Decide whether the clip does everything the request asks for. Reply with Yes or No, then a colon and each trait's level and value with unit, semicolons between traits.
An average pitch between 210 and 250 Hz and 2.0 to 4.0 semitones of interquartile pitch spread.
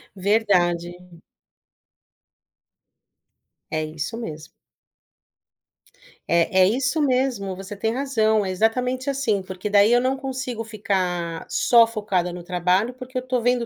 No: high, 215 Hz; wide, 5.5 semitones